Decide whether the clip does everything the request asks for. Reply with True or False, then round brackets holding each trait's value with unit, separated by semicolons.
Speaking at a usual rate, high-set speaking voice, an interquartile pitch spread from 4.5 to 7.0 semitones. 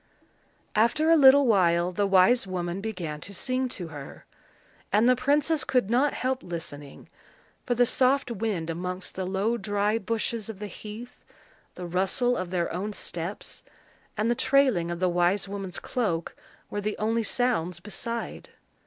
True (160 wpm; 205 Hz; 5.1 semitones)